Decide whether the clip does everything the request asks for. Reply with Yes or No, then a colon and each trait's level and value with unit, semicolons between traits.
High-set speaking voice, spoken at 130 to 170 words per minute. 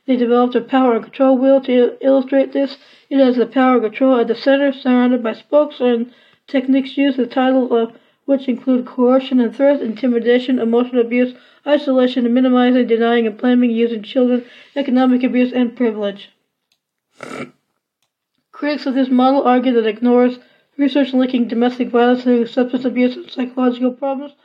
Yes: very high, 250 Hz; average, 160 wpm